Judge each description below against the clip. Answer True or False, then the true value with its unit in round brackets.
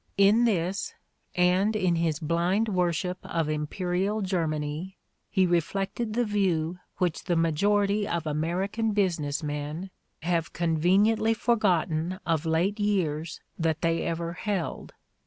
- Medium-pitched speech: True (180 Hz)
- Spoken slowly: True (125 wpm)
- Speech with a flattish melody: False (3.6 semitones)